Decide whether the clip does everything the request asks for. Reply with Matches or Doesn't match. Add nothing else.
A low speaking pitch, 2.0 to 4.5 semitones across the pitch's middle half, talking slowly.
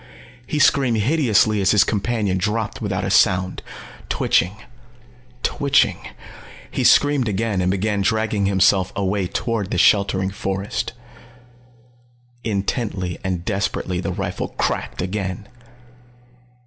Matches